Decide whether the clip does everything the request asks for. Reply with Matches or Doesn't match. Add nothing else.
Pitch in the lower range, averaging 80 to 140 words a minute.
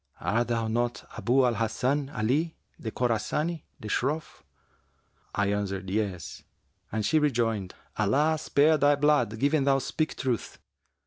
Matches